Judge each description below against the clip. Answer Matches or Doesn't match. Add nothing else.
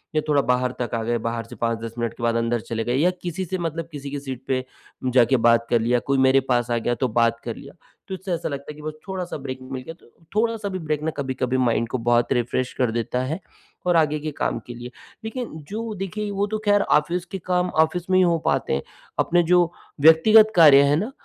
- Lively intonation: Matches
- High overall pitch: Doesn't match